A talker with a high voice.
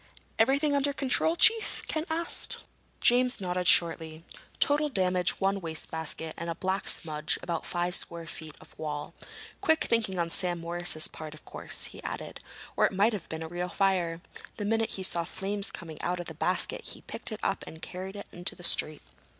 No: medium, 180 Hz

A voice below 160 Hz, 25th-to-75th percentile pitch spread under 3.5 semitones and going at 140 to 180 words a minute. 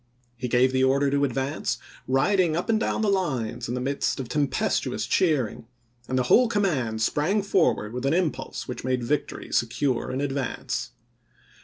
No: low, 135 Hz; average, 4.3 semitones; average, 170 wpm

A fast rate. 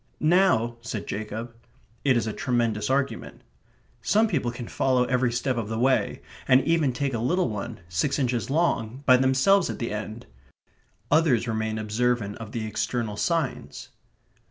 No: average, 155 wpm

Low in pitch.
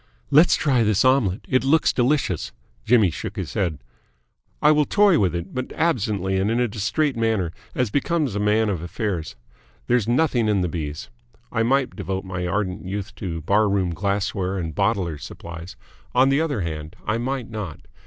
Yes: low, 105 Hz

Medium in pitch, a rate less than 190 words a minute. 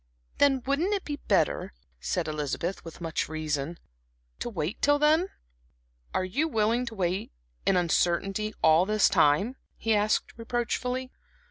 No: high, 215 Hz; average, 140 wpm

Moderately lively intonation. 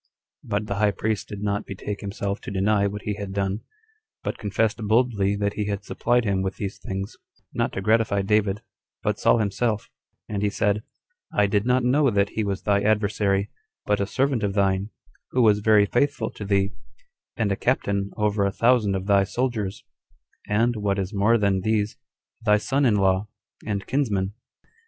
No: narrow, 1.7 semitones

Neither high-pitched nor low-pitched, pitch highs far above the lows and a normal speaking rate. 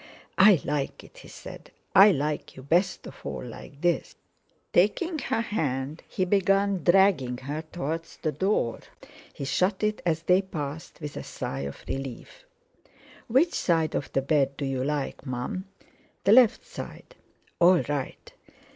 Yes: medium, 160 Hz; wide, 5.8 semitones; average, 155 wpm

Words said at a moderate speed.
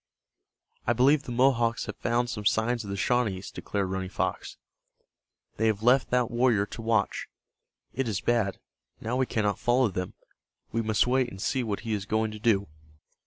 Yes: average, 180 wpm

